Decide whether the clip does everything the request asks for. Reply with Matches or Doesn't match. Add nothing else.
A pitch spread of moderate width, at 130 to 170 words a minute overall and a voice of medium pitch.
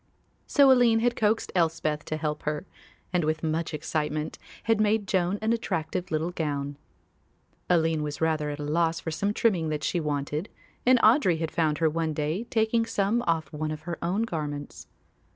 Doesn't match